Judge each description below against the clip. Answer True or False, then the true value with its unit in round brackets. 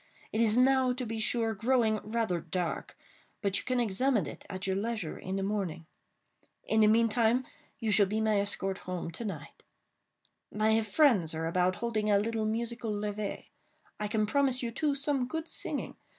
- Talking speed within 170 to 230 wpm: True (175 wpm)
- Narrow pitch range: False (3.0 semitones)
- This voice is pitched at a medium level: False (220 Hz)